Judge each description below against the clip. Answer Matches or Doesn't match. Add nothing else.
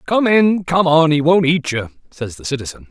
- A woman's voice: Doesn't match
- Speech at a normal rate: Doesn't match